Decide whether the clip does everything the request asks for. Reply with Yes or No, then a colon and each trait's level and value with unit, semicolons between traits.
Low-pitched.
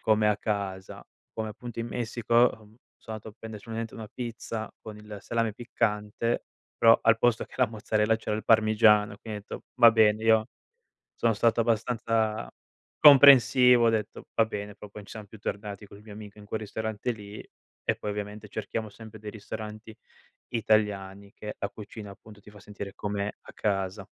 Yes: low, 110 Hz